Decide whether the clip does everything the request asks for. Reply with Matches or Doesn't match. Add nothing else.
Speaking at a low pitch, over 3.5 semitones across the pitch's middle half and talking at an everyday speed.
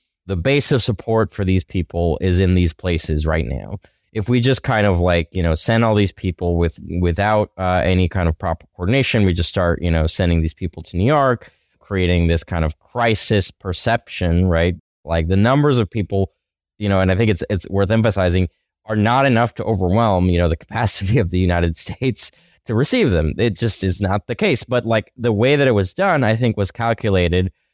Doesn't match